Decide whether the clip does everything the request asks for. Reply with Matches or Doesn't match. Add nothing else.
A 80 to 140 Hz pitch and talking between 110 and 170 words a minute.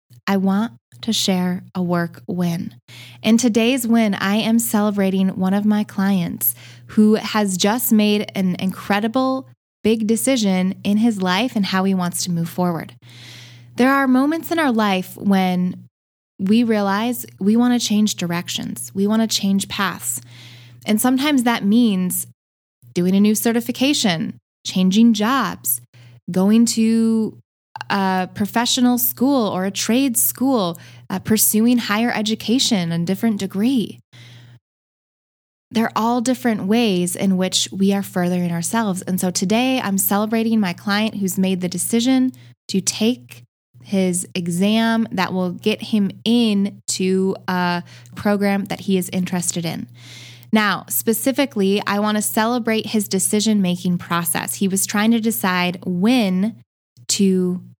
Doesn't match